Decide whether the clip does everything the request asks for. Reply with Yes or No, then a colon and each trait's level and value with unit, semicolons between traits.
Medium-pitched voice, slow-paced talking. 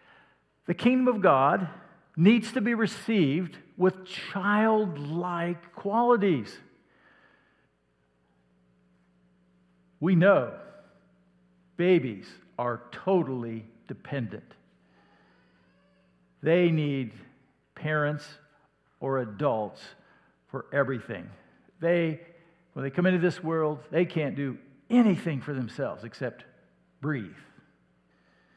Yes: medium, 150 Hz; slow, 80 wpm